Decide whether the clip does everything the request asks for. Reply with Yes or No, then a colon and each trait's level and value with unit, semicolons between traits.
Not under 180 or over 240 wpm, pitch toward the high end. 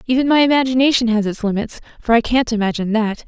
Yes: average, 200 wpm; high, 235 Hz